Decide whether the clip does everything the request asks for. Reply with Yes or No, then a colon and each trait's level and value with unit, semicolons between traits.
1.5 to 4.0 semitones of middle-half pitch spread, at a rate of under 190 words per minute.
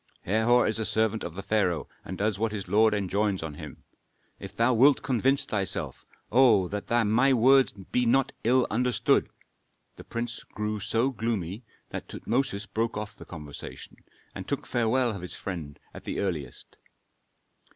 Yes: average, 3.6 semitones; average, 165 wpm